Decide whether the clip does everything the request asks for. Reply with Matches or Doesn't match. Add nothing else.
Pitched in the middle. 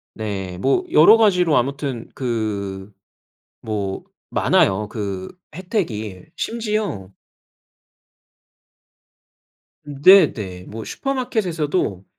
Doesn't match